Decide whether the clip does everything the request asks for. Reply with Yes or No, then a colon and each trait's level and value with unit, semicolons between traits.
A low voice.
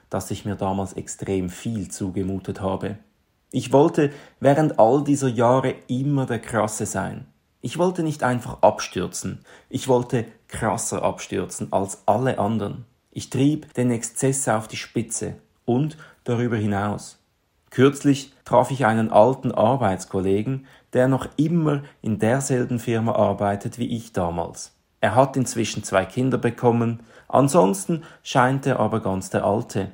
Yes: low, 120 Hz